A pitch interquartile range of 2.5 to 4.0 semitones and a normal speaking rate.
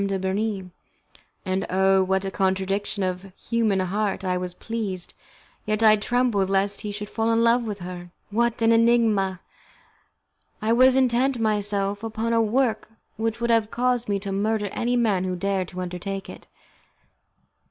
Yes: average, 3.1 semitones; average, 165 wpm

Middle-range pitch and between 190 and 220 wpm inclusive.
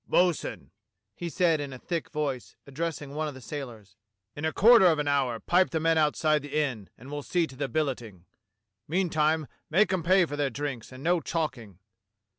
Yes: medium, 150 Hz; average, 200 wpm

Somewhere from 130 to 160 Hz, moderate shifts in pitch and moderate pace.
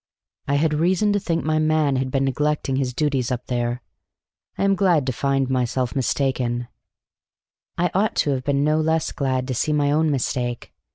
Yes: medium, 140 Hz; average, 3.4 semitones; average, 185 wpm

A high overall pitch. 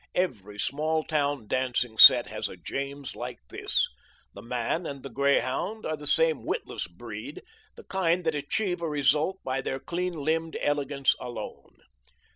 No: medium, 145 Hz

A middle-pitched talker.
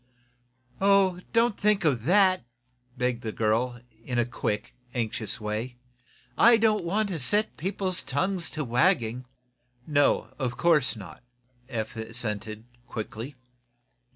No: low, 130 Hz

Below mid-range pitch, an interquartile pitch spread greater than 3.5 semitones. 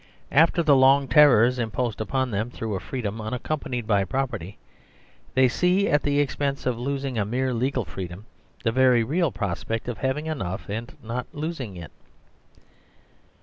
Yes: low, 125 Hz; average, 3.9 semitones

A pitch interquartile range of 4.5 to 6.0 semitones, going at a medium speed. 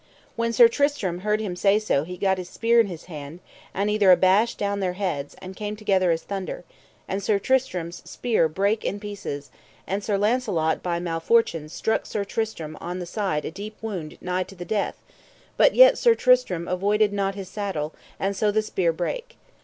No: average, 3.3 semitones; average, 195 wpm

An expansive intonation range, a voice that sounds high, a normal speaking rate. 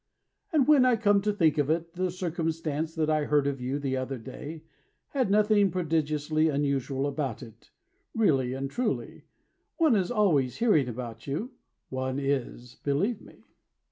No: wide, 6.3 semitones; medium, 155 Hz; average, 160 wpm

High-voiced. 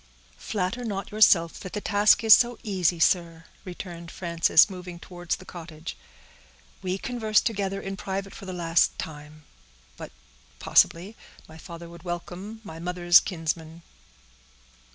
No: medium, 180 Hz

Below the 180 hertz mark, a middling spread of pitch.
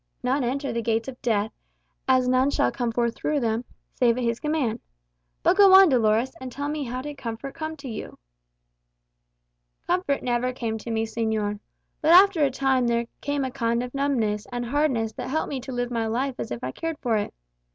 No: very high, 250 Hz; average, 3.5 semitones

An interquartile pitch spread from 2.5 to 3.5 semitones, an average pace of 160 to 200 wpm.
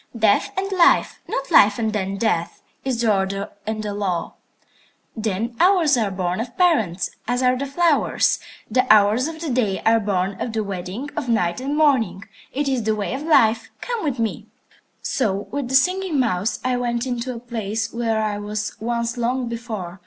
No: average, 4.2 semitones; average, 190 wpm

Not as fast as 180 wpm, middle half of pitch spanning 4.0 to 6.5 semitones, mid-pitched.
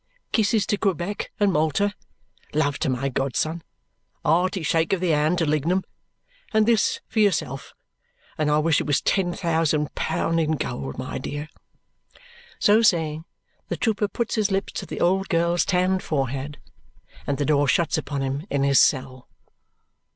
Yes: average, 165 wpm; average, 4.7 semitones; medium, 160 Hz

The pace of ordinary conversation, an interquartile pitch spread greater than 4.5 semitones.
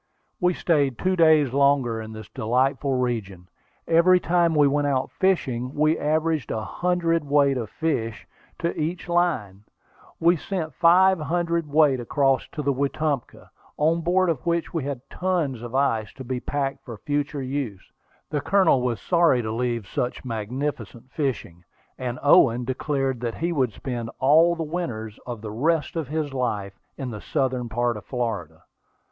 Yes: average, 165 wpm; average, 5.2 semitones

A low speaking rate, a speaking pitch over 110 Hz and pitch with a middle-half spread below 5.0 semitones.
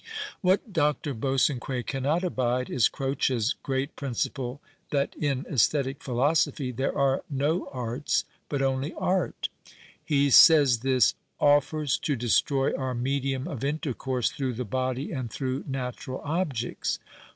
Yes: slow, 130 wpm; low, 135 Hz; narrow, 2.4 semitones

